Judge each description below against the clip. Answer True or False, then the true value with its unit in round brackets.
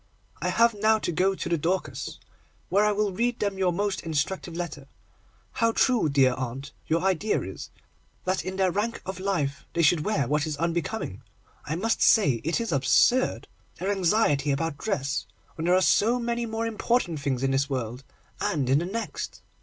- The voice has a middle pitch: True (175 Hz)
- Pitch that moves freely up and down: True (6.6 semitones)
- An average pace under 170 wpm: False (185 wpm)